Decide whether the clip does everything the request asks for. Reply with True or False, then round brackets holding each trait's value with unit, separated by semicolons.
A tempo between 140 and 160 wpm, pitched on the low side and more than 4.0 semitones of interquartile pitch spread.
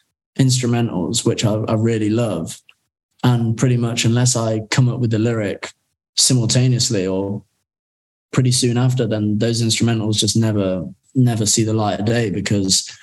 False (150 wpm; 115 Hz; 2.5 semitones)